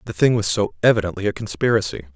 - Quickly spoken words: No, average, 195 wpm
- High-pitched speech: No, low, 100 Hz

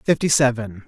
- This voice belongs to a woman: No, male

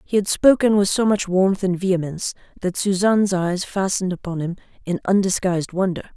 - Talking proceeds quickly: No, average, 175 wpm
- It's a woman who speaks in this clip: Yes, female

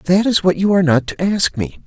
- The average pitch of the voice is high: No, medium, 180 Hz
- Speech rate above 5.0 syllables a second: Yes, 5.6 syllables/s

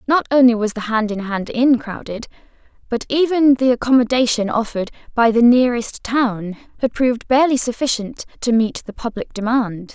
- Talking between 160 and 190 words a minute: Yes, average, 165 wpm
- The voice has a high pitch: Yes, high, 240 Hz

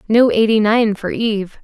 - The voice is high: Yes, high, 215 Hz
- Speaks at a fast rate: No, average, 185 wpm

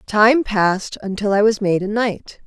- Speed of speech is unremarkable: Yes, average, 195 wpm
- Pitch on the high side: Yes, high, 205 Hz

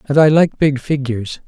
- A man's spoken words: Yes, male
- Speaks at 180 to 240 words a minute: Yes, fast, 205 wpm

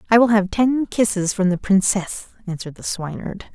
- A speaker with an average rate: Yes, average, 185 wpm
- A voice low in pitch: No, high, 200 Hz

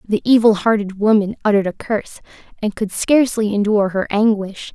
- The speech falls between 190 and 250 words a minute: No, average, 165 wpm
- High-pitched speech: Yes, high, 210 Hz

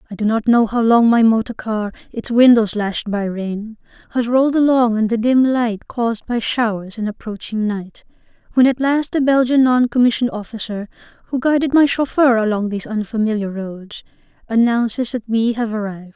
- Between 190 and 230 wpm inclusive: No, average, 175 wpm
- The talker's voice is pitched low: No, high, 230 Hz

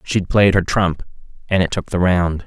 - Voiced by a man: Yes, male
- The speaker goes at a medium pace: No, fast, 220 wpm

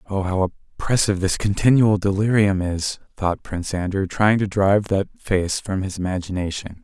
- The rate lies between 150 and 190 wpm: Yes, average, 160 wpm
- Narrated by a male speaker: Yes, male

